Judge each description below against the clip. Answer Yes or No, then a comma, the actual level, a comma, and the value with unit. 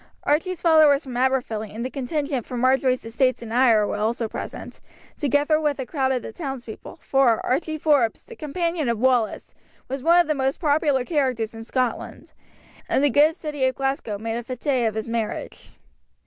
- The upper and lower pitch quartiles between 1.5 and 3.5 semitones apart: No, average, 3.9 semitones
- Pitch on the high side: Yes, very high, 265 Hz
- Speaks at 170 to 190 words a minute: Yes, average, 185 wpm